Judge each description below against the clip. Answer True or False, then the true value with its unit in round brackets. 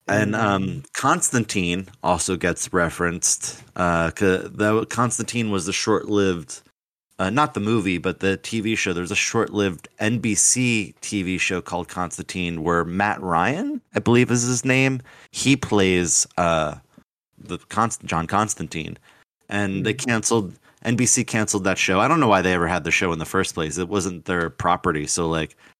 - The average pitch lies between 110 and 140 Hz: False (100 Hz)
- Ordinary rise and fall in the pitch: True (4.2 semitones)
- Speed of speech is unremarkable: True (160 wpm)